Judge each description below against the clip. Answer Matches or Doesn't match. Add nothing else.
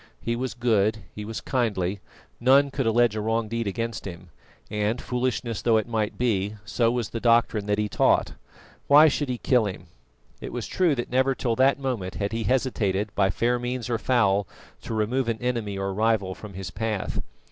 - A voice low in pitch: Matches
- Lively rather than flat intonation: Doesn't match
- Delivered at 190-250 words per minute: Matches